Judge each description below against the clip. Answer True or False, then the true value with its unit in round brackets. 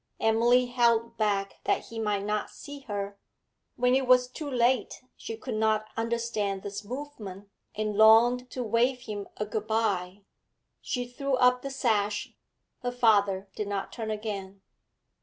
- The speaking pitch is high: True (220 Hz)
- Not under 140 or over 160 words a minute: True (155 wpm)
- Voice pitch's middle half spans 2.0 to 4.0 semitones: True (3.2 semitones)